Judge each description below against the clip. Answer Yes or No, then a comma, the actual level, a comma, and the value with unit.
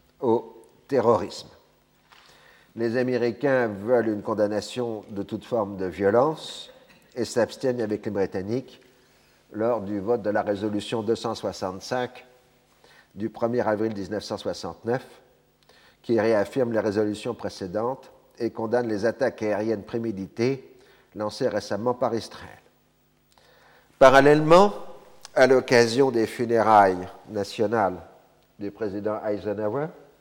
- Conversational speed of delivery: No, slow, 105 wpm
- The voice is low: Yes, low, 110 Hz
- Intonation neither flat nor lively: Yes, average, 3.3 semitones